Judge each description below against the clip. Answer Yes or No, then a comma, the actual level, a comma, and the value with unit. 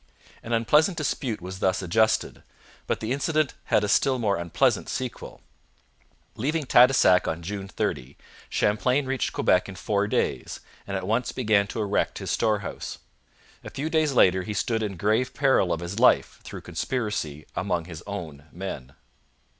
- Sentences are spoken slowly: No, average, 160 wpm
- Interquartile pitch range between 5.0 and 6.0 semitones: Yes, wide, 5.6 semitones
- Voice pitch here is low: Yes, low, 105 Hz